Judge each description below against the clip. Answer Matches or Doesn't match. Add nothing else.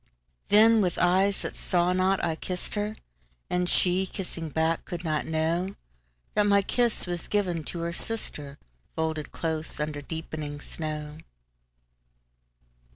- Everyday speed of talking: Doesn't match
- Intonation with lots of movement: Doesn't match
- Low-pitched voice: Doesn't match